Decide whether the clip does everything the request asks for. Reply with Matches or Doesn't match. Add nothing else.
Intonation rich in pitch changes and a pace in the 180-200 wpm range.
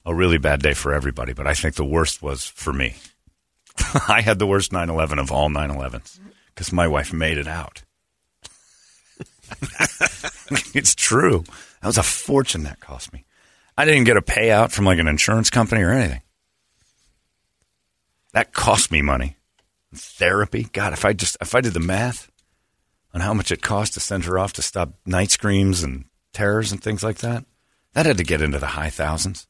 Matches